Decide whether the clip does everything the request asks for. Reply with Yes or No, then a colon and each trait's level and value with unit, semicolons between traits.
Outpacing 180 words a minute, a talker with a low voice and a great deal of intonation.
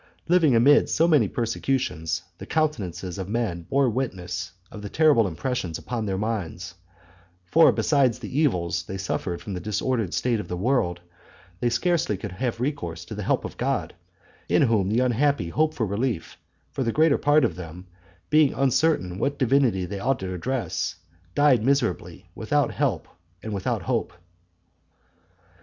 No: average, 160 wpm; low, 115 Hz; wide, 6.7 semitones